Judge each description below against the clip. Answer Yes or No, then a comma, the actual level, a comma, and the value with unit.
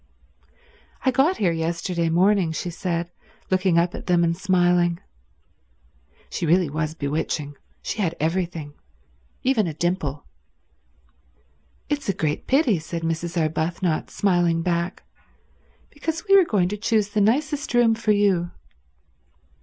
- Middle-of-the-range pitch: Yes, medium, 175 Hz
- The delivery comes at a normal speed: No, slow, 130 wpm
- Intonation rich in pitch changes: No, average, 3.8 semitones